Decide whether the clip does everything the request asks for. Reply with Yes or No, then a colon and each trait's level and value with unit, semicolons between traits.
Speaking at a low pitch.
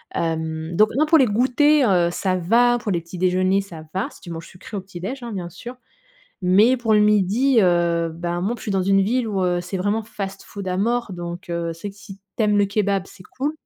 No: high, 195 Hz